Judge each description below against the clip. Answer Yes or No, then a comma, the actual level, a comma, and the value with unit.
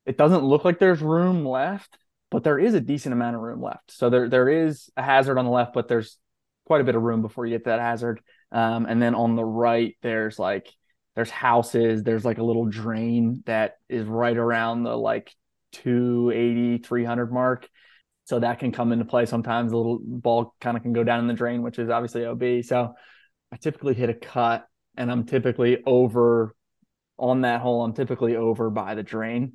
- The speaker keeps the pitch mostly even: Yes, narrow, 1.2 semitones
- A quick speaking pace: Yes, fast, 210 wpm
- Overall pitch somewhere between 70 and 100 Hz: No, low, 120 Hz